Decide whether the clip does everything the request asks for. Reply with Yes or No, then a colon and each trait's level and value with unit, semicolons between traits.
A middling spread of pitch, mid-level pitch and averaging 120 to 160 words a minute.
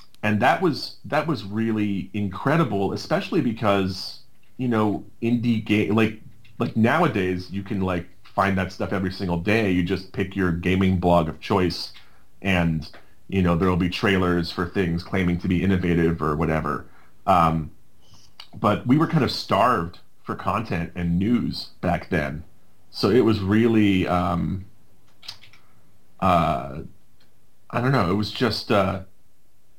No: average, 3.4 semitones; very low, 95 Hz; average, 150 wpm